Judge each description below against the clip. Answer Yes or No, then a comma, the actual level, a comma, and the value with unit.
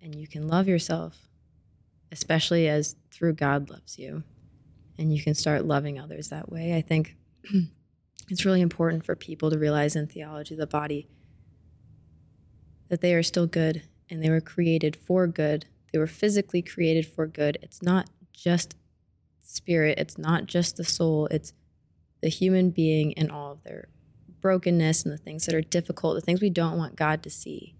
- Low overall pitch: No, medium, 160 Hz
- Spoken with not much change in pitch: Yes, narrow, 2.3 semitones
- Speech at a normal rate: Yes, average, 175 wpm